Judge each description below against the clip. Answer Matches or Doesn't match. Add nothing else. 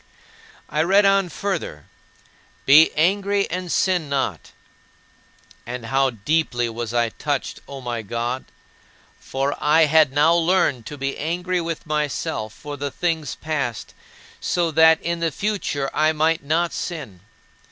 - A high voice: Doesn't match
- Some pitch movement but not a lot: Matches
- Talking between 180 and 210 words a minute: Doesn't match